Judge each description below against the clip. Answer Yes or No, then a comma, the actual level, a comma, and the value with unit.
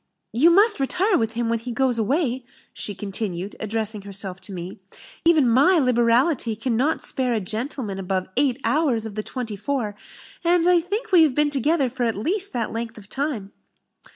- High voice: Yes, high, 240 Hz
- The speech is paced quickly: No, average, 185 wpm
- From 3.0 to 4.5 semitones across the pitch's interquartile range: No, wide, 5.6 semitones